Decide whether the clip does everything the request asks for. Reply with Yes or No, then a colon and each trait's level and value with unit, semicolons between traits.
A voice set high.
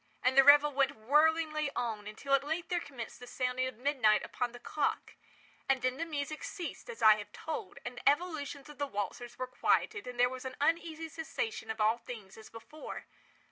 Yes: very high, 275 Hz